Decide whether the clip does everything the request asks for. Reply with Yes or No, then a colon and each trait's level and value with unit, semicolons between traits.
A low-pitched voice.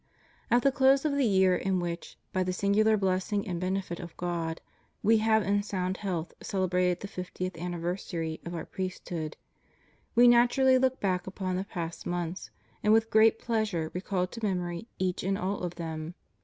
No: medium, 185 Hz